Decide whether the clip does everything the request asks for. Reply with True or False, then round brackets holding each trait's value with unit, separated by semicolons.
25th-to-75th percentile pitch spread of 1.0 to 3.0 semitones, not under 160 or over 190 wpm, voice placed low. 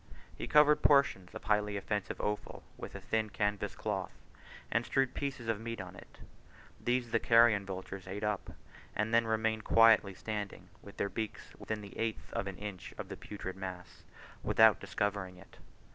True (2.5 semitones; 175 wpm; 105 Hz)